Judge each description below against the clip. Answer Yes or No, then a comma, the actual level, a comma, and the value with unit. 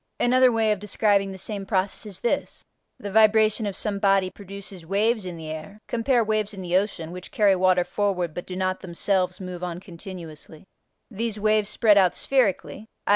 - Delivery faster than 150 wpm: Yes, average, 185 wpm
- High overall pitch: Yes, high, 195 Hz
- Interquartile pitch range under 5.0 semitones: Yes, average, 2.8 semitones